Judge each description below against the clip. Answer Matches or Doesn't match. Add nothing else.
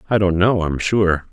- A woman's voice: Doesn't match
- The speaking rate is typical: Doesn't match